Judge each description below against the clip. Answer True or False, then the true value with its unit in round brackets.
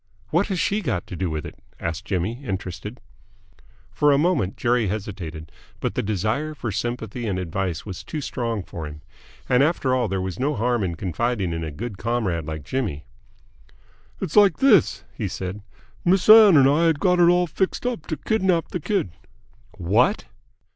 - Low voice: True (120 Hz)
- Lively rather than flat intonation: True (9.0 semitones)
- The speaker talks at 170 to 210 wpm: True (180 wpm)